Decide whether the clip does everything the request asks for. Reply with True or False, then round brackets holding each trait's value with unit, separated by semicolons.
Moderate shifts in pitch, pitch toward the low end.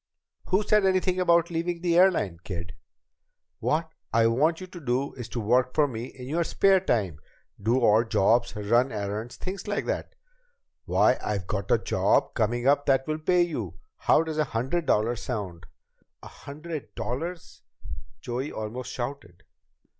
False (7.1 semitones; 130 Hz)